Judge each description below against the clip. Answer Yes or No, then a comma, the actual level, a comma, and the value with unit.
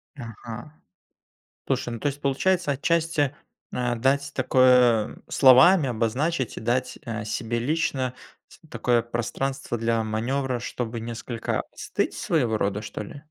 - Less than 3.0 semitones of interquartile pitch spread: No, average, 3.3 semitones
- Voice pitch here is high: No, low, 125 Hz